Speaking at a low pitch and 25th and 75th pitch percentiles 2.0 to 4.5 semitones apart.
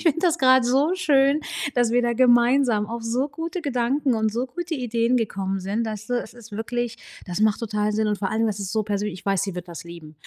No: high, 230 Hz; average, 3.8 semitones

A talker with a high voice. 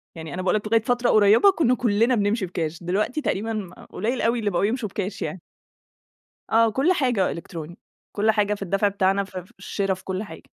Yes: high, 205 Hz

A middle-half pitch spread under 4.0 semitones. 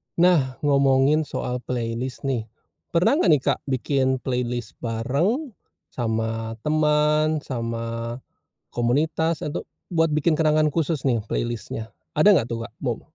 No: average, 4.6 semitones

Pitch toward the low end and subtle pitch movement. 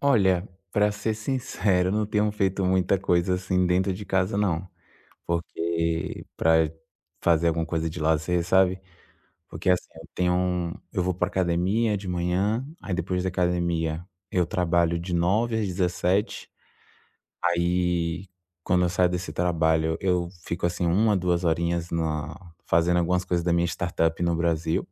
Yes: very low, 90 Hz; narrow, 1.7 semitones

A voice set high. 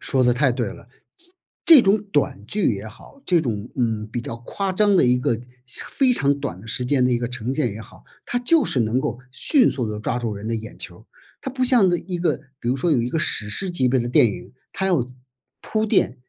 No: low, 130 Hz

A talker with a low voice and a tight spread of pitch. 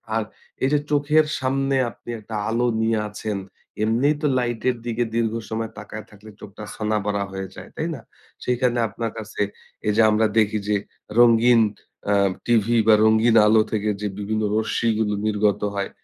Yes: low, 110 Hz; narrow, 2.1 semitones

